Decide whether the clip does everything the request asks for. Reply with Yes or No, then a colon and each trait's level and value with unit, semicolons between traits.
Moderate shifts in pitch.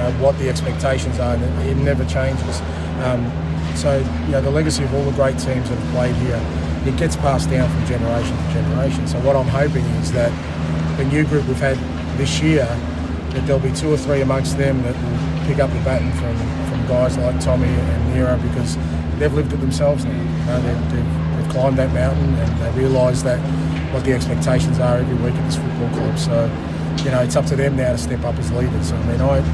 No: wide, 7.8 semitones